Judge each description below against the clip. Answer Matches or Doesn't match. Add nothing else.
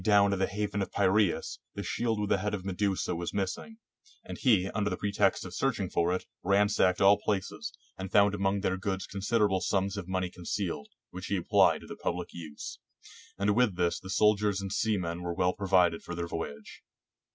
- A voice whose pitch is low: Matches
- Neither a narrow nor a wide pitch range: Doesn't match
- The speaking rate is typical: Matches